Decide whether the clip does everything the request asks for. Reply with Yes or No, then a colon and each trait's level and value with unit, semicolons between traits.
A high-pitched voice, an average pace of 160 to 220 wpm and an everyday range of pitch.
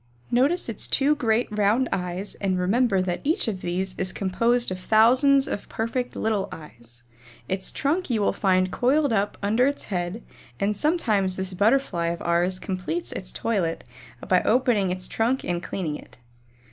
Yes: high, 205 Hz; average, 165 wpm; average, 5.0 semitones